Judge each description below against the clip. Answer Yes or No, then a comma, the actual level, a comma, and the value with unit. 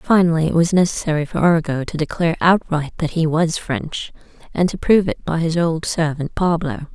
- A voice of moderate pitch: Yes, medium, 165 Hz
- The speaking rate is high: No, average, 190 wpm